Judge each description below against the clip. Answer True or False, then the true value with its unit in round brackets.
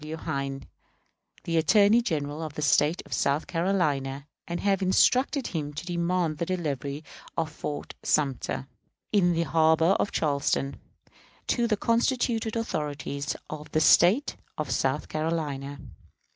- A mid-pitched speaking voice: True (160 Hz)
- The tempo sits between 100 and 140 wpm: True (135 wpm)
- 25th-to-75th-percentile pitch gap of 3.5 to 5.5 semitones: True (4.2 semitones)